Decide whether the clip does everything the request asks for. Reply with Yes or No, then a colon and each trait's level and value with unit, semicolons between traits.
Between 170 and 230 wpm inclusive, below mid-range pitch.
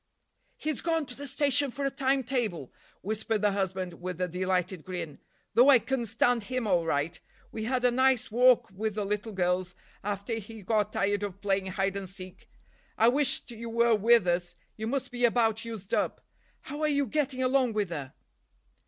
No: average, 190 wpm; high, 220 Hz